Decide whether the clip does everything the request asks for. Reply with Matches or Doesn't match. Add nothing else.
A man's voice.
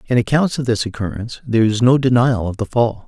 Matches